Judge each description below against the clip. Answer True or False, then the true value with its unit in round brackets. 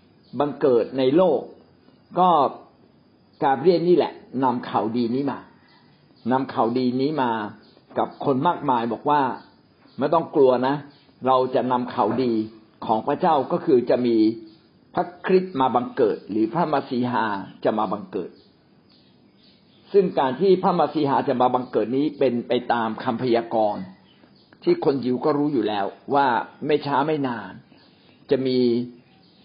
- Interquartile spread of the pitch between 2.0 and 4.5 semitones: True (3.9 semitones)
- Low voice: True (130 Hz)